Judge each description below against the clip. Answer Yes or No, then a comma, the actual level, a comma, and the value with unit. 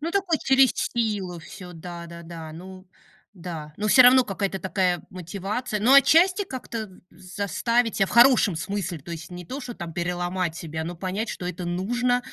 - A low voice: No, high, 190 Hz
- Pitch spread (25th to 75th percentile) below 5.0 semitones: No, wide, 5.6 semitones